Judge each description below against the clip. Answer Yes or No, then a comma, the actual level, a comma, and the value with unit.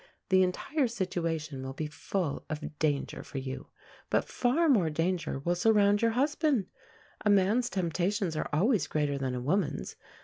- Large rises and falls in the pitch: Yes, wide, 6.0 semitones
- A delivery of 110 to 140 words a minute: No, average, 160 wpm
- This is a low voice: No, medium, 180 Hz